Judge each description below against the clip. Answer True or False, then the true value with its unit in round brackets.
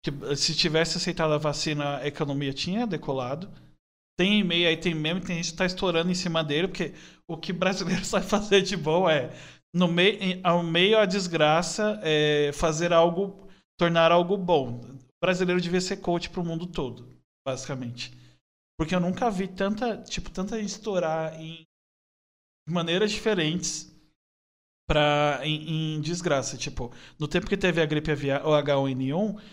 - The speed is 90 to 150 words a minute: False (165 wpm)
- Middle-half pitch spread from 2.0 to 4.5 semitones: True (3.9 semitones)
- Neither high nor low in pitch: True (165 Hz)